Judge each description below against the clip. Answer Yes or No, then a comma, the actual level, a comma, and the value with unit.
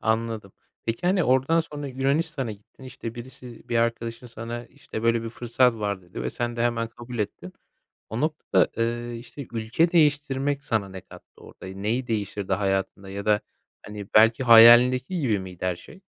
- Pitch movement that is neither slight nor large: Yes, average, 3.5 semitones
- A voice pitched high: No, low, 115 Hz